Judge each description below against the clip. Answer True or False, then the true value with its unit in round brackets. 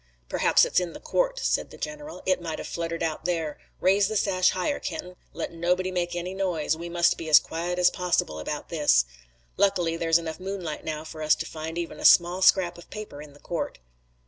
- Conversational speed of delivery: False (215 wpm)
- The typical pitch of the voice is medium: True (175 Hz)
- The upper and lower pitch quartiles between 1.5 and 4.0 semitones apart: True (2.4 semitones)